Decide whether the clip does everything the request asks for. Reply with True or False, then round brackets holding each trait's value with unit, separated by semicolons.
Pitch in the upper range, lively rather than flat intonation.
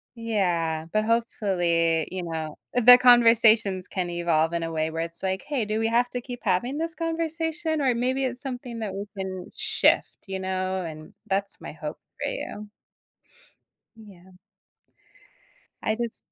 True (210 Hz; 5.8 semitones)